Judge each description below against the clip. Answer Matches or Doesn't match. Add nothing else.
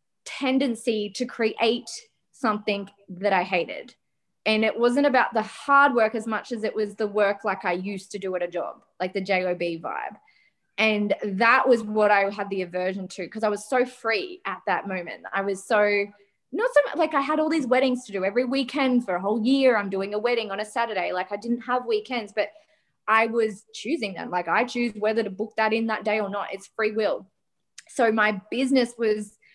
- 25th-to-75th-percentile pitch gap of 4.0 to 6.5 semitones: Doesn't match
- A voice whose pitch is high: Matches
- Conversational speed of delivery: Doesn't match